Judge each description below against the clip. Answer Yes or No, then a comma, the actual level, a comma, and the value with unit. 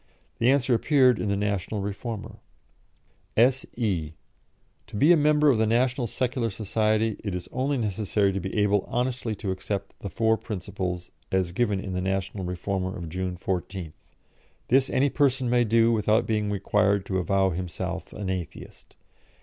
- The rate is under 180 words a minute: Yes, average, 160 wpm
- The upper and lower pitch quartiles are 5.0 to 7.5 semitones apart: No, average, 4.0 semitones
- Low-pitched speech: Yes, low, 105 Hz